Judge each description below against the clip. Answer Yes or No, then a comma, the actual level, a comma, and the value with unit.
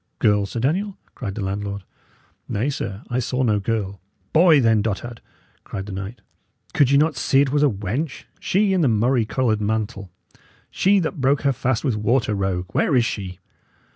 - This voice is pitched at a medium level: No, low, 115 Hz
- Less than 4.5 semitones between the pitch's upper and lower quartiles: No, average, 5.2 semitones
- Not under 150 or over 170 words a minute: No, average, 185 wpm